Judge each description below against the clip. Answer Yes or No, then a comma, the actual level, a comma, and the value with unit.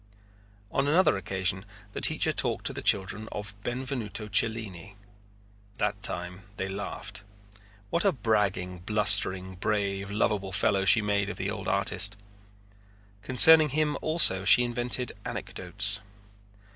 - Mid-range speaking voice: No, low, 105 Hz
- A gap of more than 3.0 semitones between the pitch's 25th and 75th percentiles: Yes, average, 3.4 semitones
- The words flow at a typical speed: No, slow, 125 wpm